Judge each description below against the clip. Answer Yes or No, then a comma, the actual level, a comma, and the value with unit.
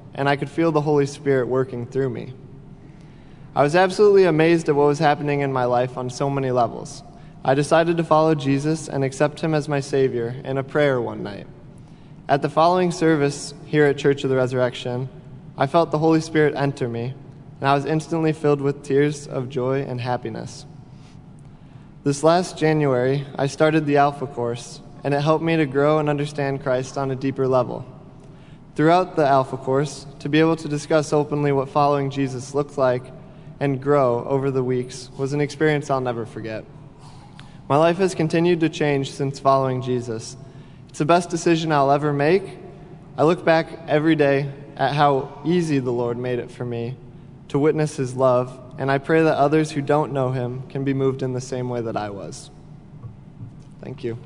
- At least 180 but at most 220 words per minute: Yes, average, 190 wpm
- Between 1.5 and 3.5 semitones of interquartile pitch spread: Yes, average, 2.7 semitones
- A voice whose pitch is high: No, medium, 140 Hz